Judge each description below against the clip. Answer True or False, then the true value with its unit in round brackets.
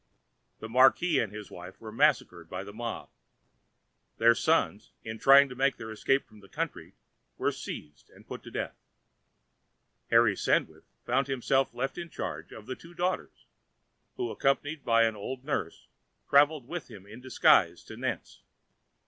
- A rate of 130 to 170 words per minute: True (160 wpm)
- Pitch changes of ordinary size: True (4.4 semitones)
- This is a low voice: True (125 Hz)